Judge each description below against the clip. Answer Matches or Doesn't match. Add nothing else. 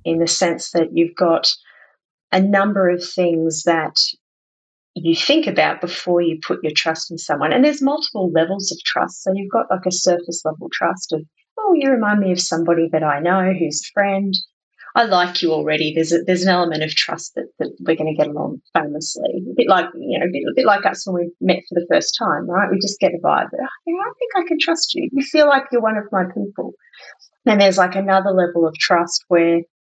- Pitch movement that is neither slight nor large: Matches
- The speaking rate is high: Matches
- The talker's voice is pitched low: Doesn't match